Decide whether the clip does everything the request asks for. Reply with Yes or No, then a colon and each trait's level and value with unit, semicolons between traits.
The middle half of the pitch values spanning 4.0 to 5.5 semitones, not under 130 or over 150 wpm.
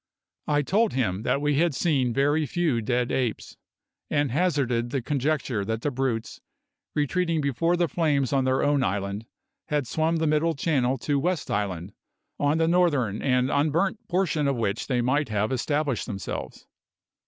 No: average, 4.5 semitones; average, 165 wpm